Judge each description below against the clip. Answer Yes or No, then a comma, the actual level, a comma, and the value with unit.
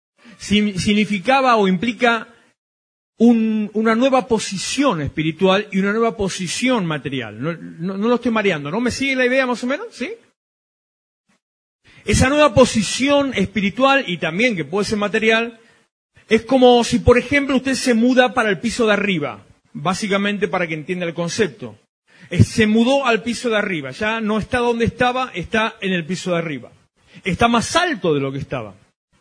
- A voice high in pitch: Yes, high, 220 Hz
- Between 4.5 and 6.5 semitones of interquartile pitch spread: Yes, average, 4.8 semitones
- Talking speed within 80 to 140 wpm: No, average, 170 wpm